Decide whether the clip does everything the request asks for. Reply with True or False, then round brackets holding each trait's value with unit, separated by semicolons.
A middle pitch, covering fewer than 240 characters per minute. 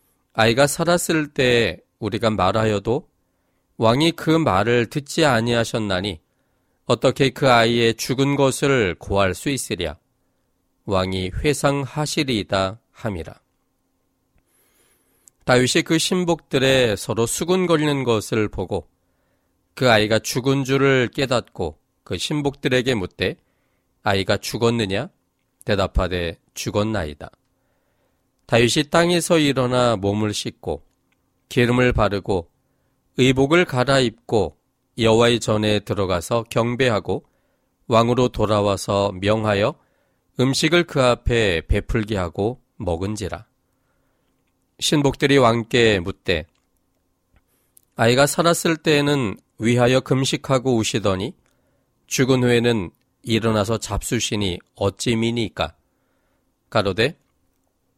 False (115 Hz; 230 characters per minute)